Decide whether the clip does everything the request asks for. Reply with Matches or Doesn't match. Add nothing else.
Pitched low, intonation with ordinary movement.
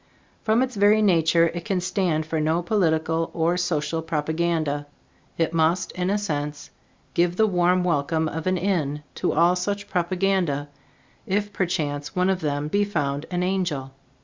Doesn't match